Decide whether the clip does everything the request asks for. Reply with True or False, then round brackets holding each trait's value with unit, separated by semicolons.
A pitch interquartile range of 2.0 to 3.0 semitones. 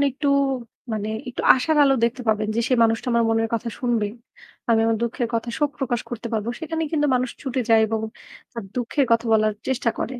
True (2.7 semitones)